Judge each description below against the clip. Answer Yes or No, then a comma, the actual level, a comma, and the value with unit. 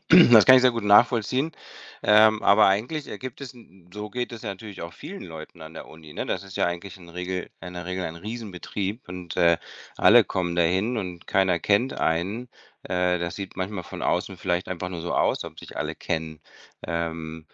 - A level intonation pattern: No, average, 4.0 semitones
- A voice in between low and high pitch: No, very low, 95 Hz